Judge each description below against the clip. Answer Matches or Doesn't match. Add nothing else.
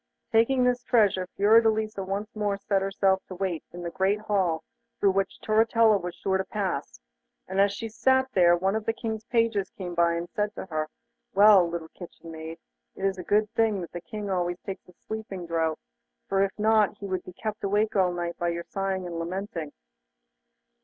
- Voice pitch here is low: Doesn't match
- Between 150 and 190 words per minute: Doesn't match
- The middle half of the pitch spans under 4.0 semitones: Matches